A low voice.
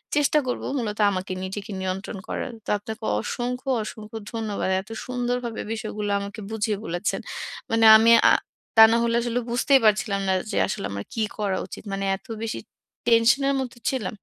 No: high, 220 Hz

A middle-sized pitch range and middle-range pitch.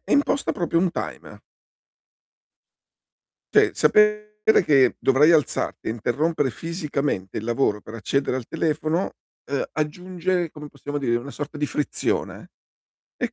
Yes: average, 4.3 semitones; medium, 150 Hz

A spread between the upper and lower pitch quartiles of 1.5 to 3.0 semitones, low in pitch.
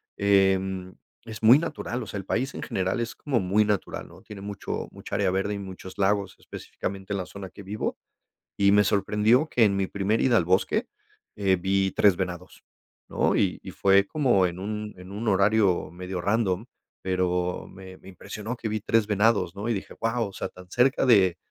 Yes: narrow, 2.4 semitones; low, 100 Hz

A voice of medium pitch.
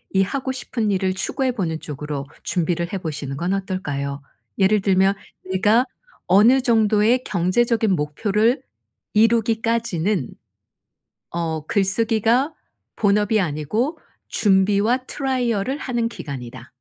No: high, 200 Hz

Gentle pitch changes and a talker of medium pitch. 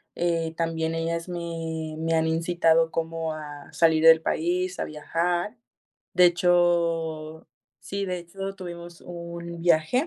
Yes: narrow, 1.3 semitones; medium, 165 Hz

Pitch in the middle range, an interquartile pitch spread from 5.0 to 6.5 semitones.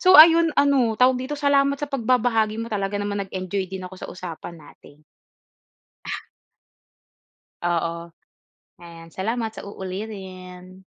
No: high, 205 Hz; wide, 5.6 semitones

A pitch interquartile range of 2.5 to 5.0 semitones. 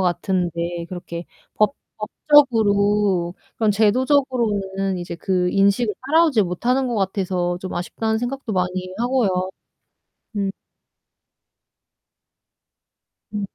Yes: average, 4.3 semitones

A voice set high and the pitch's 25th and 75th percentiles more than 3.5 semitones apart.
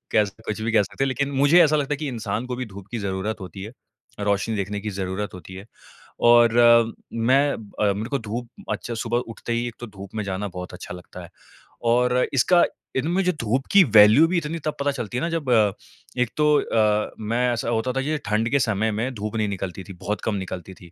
No: low, 115 Hz; average, 4.5 semitones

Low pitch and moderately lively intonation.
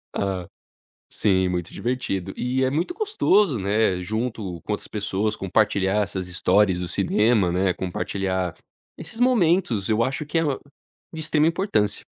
No: low, 105 Hz; wide, 5.8 semitones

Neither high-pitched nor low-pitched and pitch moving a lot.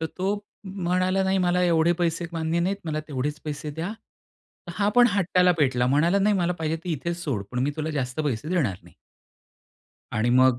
No: medium, 165 Hz; average, 3.7 semitones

